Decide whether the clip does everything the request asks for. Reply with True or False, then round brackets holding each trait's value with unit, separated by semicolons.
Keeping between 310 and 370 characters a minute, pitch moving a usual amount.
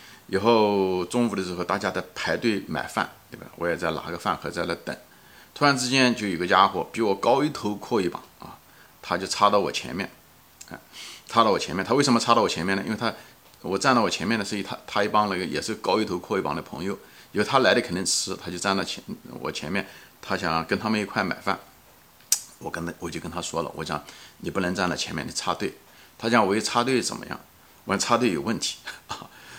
True (315 characters per minute; 3.7 semitones)